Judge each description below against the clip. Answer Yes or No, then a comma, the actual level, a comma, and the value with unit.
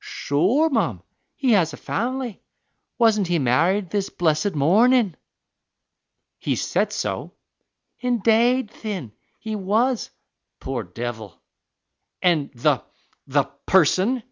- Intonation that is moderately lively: No, wide, 7.5 semitones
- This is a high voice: Yes, high, 195 Hz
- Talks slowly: Yes, slow, 110 wpm